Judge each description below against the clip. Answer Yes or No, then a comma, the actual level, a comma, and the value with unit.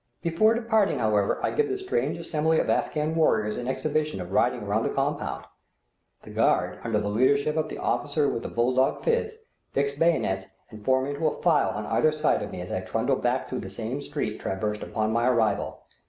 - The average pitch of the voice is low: Yes, low, 130 Hz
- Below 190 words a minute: No, fast, 205 wpm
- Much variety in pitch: Yes, wide, 6.2 semitones